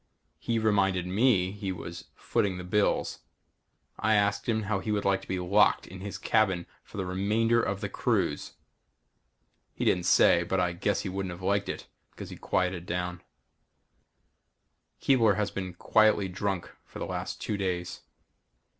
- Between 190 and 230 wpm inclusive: No, average, 165 wpm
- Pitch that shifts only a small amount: Yes, narrow, 2.3 semitones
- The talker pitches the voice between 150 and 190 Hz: No, very low, 95 Hz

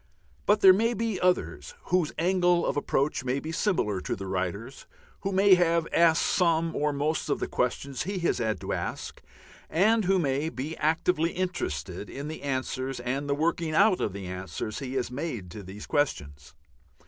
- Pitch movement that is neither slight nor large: No, wide, 6.1 semitones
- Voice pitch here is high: No, medium, 155 Hz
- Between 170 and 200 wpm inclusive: Yes, average, 185 wpm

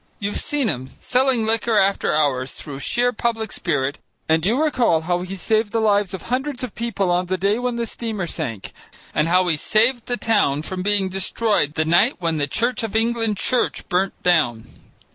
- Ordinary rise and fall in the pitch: No, wide, 5.8 semitones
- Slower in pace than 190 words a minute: No, average, 195 wpm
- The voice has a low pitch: No, high, 200 Hz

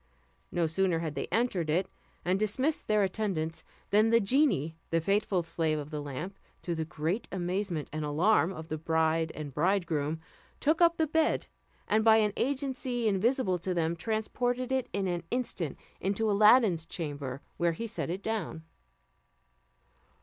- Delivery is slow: No, average, 160 wpm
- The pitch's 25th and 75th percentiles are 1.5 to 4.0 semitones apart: No, wide, 5.5 semitones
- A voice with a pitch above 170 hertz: Yes, medium, 185 Hz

